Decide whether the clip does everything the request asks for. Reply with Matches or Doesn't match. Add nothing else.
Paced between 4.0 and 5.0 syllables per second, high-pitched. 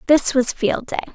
Matches